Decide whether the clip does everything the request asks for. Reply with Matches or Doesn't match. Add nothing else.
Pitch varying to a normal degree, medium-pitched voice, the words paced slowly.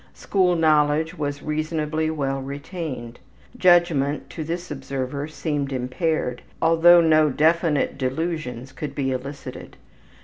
Matches